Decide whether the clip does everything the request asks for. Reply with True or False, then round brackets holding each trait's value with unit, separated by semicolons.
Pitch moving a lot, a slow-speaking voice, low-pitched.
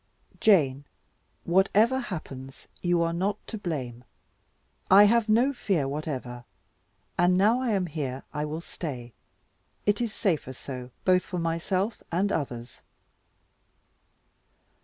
False (6.8 semitones; 120 wpm; 170 Hz)